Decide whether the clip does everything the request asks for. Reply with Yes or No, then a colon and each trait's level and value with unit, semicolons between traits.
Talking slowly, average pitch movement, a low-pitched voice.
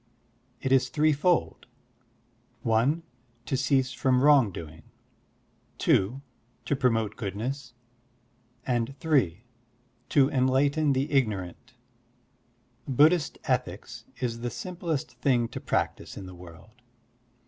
Yes: slow, 105 wpm; average, 4.0 semitones; low, 130 Hz